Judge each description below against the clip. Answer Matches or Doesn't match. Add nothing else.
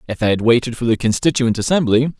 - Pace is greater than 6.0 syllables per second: Matches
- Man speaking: Matches